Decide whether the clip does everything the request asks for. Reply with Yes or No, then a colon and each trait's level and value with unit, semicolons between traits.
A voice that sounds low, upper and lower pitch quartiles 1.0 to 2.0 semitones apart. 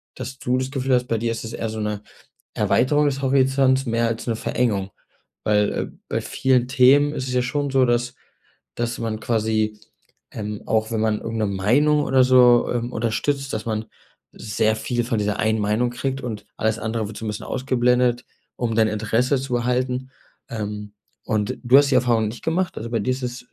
No: low, 120 Hz; average, 2.8 semitones